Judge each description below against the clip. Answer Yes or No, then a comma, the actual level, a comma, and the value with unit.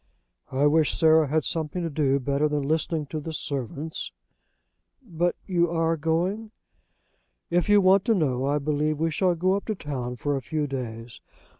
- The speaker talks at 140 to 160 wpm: No, average, 175 wpm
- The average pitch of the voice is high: No, medium, 155 Hz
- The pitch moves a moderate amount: Yes, average, 3.2 semitones